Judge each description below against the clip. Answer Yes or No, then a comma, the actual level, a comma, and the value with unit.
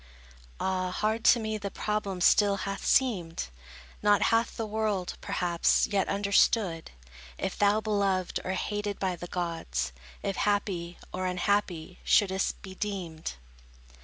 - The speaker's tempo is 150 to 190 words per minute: No, slow, 135 wpm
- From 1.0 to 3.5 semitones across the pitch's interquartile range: Yes, narrow, 2.4 semitones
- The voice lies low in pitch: No, high, 195 Hz